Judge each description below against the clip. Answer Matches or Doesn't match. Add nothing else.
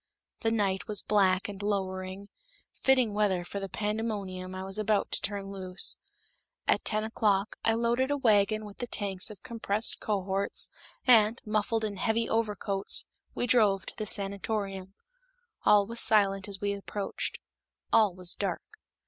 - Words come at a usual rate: Matches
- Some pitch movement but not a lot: Doesn't match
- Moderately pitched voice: Doesn't match